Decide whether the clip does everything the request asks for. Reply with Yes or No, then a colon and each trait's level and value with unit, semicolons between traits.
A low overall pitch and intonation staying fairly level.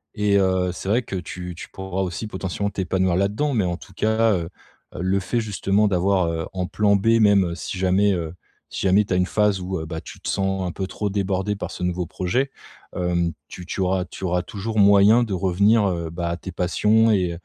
Yes: very low, 95 Hz; narrow, 2.3 semitones